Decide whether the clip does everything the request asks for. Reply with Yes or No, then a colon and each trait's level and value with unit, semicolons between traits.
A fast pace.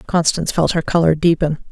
No: average, 175 wpm